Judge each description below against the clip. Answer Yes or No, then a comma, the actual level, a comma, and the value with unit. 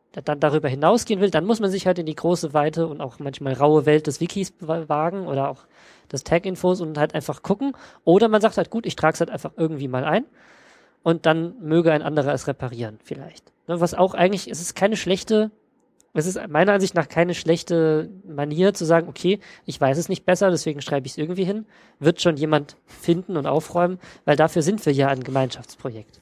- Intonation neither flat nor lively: Yes, average, 4.0 semitones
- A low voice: No, medium, 165 Hz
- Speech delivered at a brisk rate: Yes, fast, 210 wpm